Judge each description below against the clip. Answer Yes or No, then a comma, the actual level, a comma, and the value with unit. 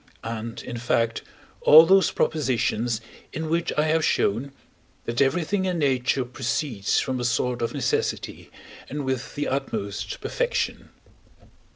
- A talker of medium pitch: No, low, 130 Hz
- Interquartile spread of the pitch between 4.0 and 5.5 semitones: Yes, average, 4.8 semitones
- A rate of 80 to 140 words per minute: Yes, slow, 135 wpm